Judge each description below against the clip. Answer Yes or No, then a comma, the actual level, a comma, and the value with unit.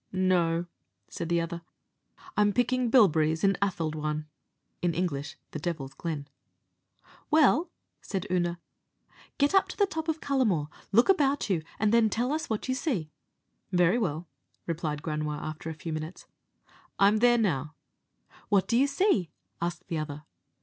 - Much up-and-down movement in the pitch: Yes, wide, 7.2 semitones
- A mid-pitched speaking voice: Yes, medium, 180 Hz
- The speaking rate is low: No, average, 150 wpm